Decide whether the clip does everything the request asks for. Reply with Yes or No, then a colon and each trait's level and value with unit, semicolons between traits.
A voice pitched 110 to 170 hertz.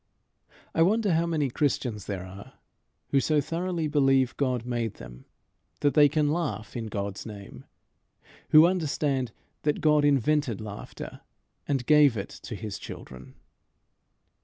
Yes: low, 135 Hz